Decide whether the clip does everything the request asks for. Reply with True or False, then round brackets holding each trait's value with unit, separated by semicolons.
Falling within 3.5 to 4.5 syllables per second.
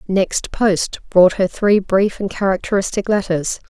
True (4.1 syllables/s)